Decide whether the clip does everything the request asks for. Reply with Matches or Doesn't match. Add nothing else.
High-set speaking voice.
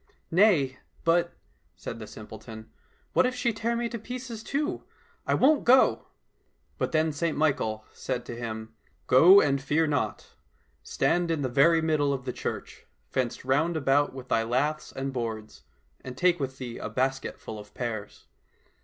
Doesn't match